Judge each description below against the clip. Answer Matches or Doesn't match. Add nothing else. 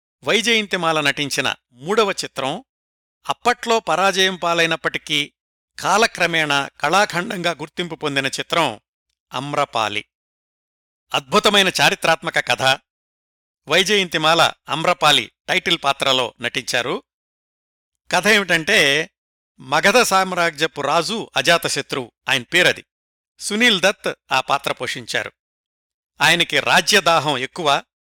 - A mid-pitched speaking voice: Matches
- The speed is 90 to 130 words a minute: Doesn't match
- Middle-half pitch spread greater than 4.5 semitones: Matches